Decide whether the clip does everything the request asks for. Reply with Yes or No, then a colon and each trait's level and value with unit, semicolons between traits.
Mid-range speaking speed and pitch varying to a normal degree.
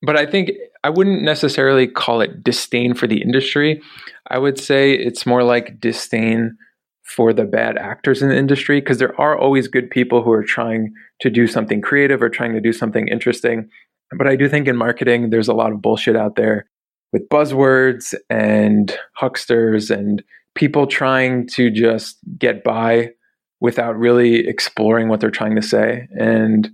Yes: average, 175 wpm; average, 3.0 semitones